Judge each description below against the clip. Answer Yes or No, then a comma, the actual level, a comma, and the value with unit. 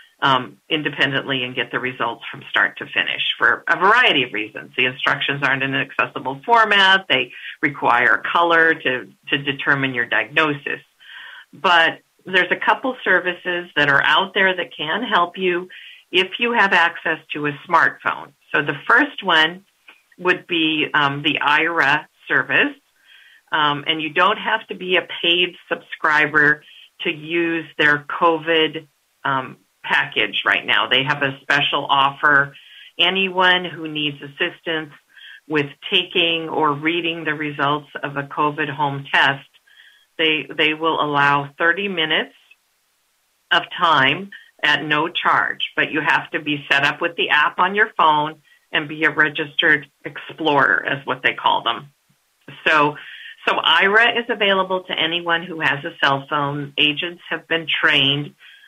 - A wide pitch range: No, average, 3.8 semitones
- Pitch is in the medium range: Yes, medium, 160 Hz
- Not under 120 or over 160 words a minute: Yes, average, 150 wpm